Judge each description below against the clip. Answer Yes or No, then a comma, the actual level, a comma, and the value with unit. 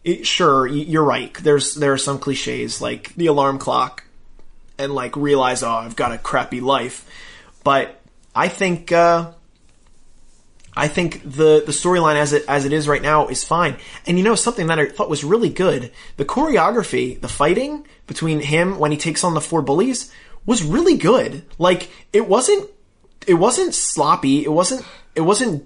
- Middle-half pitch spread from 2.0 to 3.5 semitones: No, average, 4.1 semitones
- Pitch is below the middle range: No, medium, 155 Hz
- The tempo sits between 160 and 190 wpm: Yes, average, 180 wpm